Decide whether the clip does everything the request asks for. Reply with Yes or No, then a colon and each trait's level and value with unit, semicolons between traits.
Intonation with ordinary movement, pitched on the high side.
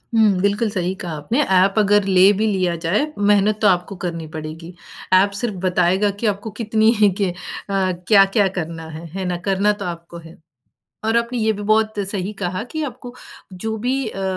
Yes: average, 3.1 semitones; high, 195 Hz